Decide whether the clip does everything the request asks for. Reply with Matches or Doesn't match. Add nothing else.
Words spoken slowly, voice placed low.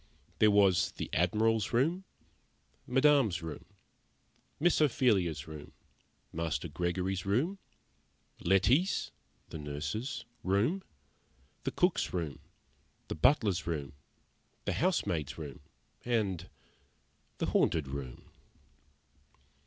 Matches